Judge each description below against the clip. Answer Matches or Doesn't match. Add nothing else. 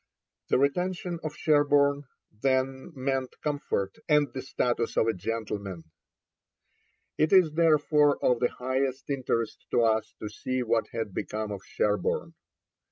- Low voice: Matches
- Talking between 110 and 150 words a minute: Matches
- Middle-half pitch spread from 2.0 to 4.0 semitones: Doesn't match